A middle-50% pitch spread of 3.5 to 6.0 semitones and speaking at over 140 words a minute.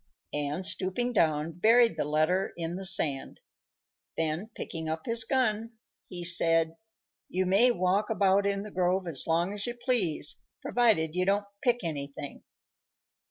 Yes: average, 4.7 semitones; average, 150 wpm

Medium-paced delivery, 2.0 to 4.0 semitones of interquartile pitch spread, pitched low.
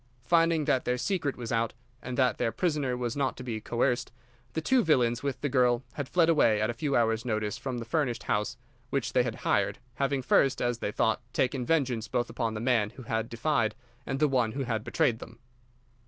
No: fast, 215 wpm; average, 3.3 semitones; low, 125 Hz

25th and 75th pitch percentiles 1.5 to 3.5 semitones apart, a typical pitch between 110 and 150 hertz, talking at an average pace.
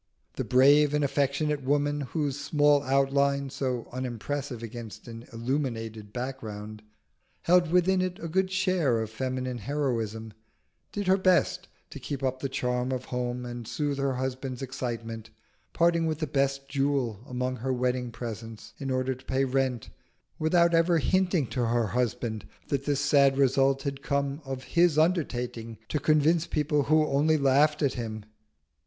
Yes: average, 3.2 semitones; low, 135 Hz; average, 155 wpm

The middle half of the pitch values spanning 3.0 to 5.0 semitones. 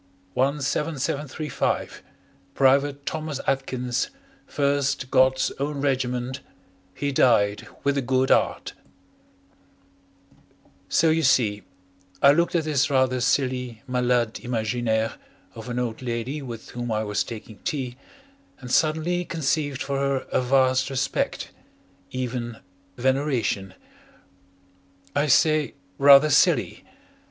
No: narrow, 2.6 semitones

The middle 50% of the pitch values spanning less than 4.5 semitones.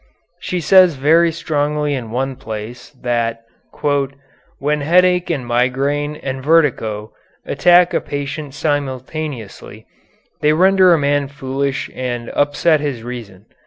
Yes: average, 3.8 semitones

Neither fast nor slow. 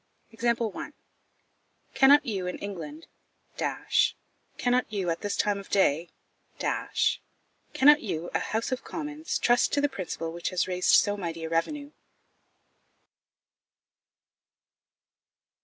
No: slow, 105 wpm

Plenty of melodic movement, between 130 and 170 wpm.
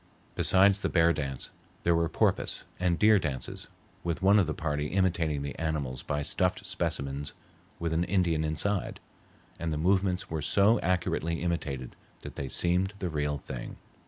No: average, 3.9 semitones; average, 160 wpm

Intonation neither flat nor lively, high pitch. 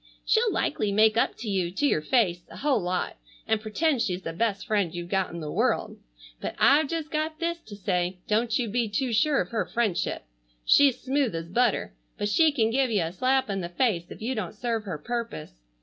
No: wide, 5.9 semitones; high, 220 Hz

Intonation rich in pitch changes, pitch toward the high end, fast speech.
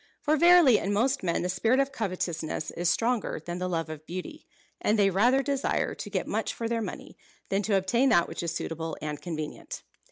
Yes: wide, 6.6 semitones; high, 195 Hz; fast, 210 wpm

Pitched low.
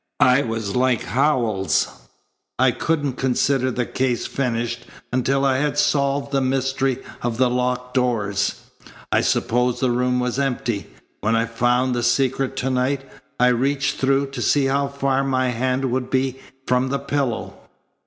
Yes: low, 130 Hz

